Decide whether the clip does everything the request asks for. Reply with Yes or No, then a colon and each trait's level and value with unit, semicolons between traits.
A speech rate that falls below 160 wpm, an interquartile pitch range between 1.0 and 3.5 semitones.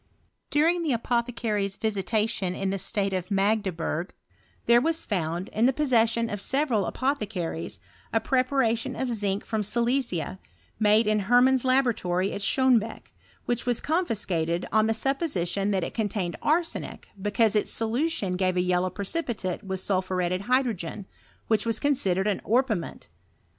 No: average, 150 wpm; average, 4.6 semitones